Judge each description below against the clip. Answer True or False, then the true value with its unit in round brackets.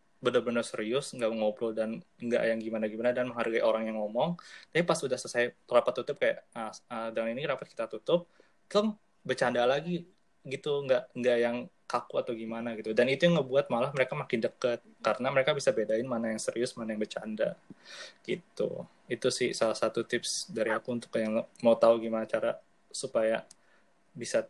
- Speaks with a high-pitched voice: False (115 Hz)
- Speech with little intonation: True (2.1 semitones)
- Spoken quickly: True (175 wpm)